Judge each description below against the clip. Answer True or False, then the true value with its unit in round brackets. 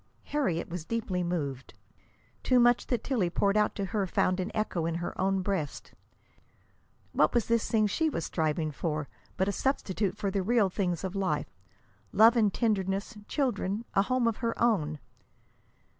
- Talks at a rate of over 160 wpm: True (170 wpm)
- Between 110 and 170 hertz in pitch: False (195 Hz)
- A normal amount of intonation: True (4.6 semitones)